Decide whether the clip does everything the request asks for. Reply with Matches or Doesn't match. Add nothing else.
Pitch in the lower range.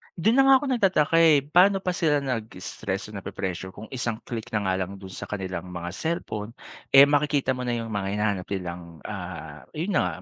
Matches